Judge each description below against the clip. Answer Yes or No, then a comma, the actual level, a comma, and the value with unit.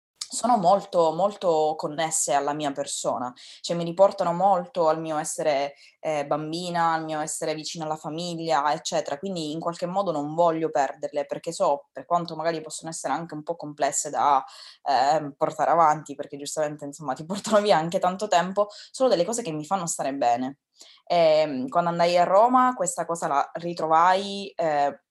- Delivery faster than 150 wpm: Yes, fast, 170 wpm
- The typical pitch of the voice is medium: Yes, medium, 165 Hz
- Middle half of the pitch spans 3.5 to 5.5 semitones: No, average, 2.8 semitones